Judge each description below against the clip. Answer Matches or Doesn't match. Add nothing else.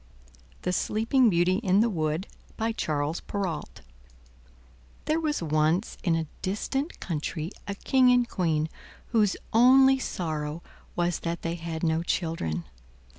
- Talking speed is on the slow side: Matches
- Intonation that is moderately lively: Doesn't match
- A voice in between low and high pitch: Matches